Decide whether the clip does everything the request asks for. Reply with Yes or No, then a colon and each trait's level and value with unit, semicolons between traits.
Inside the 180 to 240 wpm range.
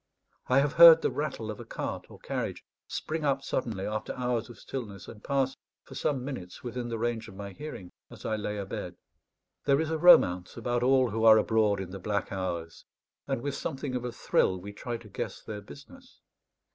Yes: fast, 205 wpm